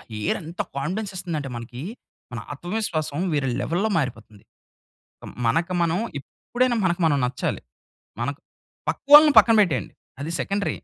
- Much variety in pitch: Yes, wide, 6.4 semitones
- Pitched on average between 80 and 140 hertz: No, medium, 165 Hz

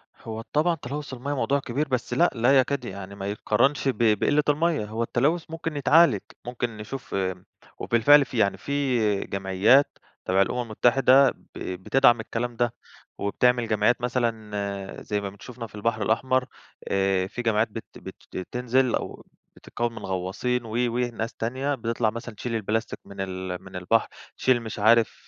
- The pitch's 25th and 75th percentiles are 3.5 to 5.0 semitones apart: Yes, average, 3.8 semitones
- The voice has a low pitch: Yes, low, 115 Hz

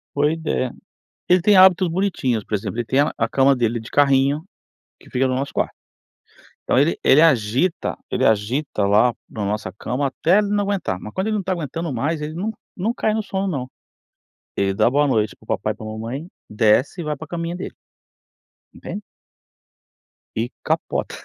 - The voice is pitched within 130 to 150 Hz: Yes, medium, 140 Hz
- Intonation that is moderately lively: No, wide, 7.1 semitones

